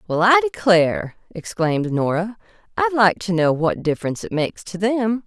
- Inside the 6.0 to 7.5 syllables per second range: No, 5.3 syllables/s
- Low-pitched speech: No, high, 195 Hz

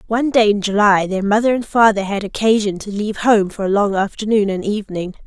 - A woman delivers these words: Yes, female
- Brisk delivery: Yes, fast, 215 wpm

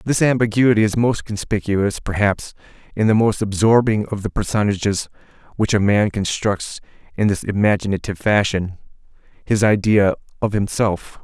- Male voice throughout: Yes, male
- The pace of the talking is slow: Yes, slow, 130 wpm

